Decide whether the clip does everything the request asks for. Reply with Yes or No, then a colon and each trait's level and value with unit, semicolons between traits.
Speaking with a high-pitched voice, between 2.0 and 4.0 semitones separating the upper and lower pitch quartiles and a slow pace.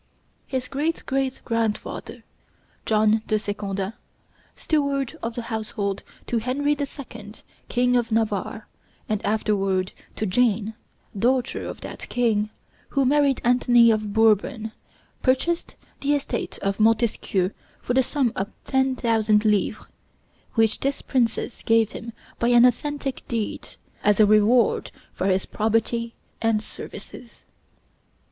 Yes: high, 230 Hz; average, 3.0 semitones; slow, 125 wpm